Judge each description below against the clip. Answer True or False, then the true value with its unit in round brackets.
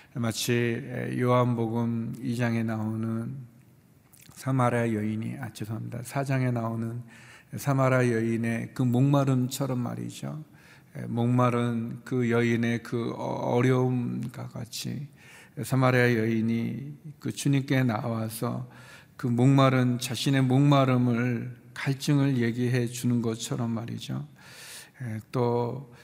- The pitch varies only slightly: True (2.2 semitones)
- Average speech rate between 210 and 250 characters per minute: True (225 characters per minute)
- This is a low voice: True (120 Hz)